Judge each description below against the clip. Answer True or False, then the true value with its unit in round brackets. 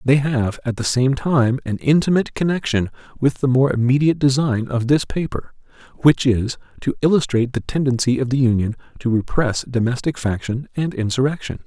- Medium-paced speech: True (165 wpm)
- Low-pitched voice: True (130 Hz)